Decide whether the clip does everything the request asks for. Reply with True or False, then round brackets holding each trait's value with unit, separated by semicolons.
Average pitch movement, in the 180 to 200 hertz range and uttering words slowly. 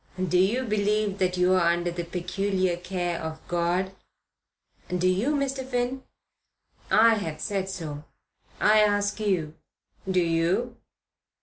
True (3.4 semitones; 185 Hz; 125 wpm)